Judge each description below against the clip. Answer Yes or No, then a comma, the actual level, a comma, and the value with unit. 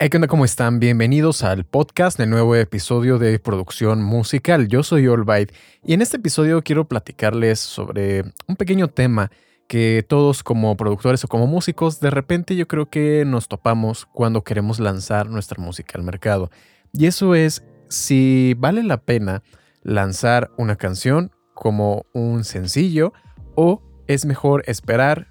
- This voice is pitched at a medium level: No, low, 120 Hz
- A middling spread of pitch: No, wide, 6.1 semitones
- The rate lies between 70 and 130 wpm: No, average, 150 wpm